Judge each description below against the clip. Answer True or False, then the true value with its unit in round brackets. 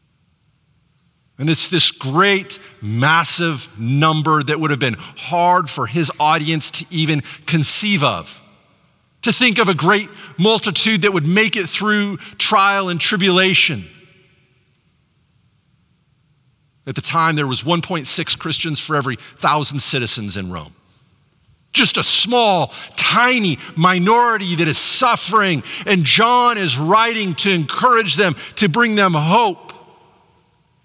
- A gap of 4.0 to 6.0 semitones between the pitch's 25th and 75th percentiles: True (5.5 semitones)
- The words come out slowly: True (125 wpm)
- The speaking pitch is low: False (165 Hz)